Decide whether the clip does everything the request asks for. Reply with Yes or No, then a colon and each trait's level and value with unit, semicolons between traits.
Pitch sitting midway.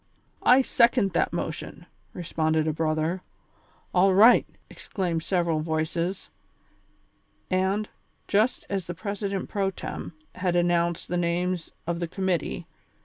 Yes: medium, 175 Hz